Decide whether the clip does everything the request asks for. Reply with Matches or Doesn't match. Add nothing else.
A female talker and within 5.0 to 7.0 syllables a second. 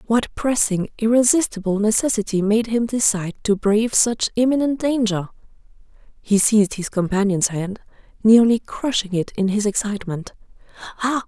Matches